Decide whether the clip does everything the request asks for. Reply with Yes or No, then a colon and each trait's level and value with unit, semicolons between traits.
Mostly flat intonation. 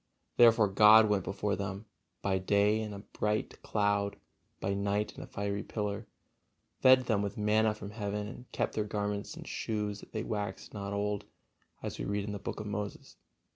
Yes: narrow, 1.0 semitones